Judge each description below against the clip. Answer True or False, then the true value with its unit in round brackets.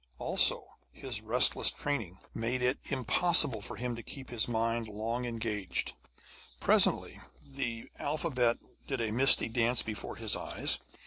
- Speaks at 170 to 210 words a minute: False (135 wpm)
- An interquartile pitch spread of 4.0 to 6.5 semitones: False (2.5 semitones)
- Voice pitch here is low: True (120 Hz)